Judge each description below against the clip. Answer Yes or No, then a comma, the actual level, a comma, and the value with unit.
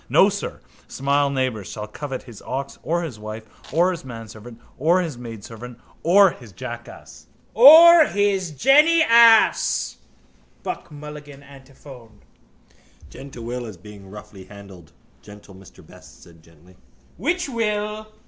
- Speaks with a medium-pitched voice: No, low, 130 Hz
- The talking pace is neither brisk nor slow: No, slow, 130 wpm